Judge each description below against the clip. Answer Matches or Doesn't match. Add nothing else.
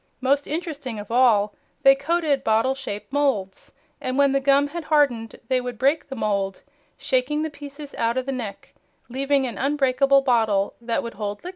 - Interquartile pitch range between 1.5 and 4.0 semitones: Matches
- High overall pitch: Matches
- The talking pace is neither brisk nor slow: Matches